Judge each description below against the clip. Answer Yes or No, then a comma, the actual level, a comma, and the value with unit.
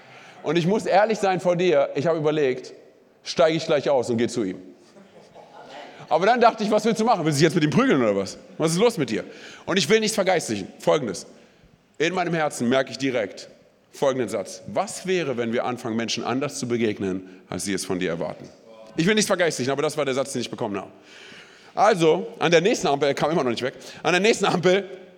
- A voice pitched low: No, medium, 145 Hz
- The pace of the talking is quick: Yes, fast, 230 wpm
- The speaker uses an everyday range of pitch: No, wide, 7.6 semitones